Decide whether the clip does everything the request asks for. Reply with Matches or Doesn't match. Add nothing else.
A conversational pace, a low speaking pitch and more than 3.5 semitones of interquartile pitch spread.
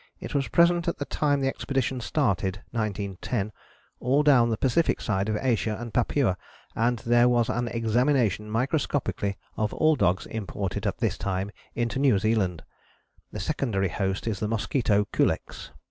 Matches